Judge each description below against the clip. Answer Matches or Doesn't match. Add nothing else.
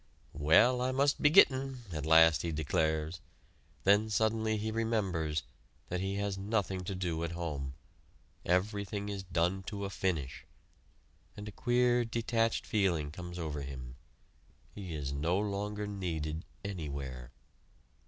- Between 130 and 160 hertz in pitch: Doesn't match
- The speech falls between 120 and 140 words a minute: Matches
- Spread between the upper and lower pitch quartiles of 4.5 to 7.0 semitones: Matches